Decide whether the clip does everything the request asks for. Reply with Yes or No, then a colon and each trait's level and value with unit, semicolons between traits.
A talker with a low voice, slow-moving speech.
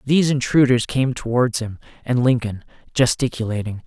Yes: low, 125 Hz; slow, 125 wpm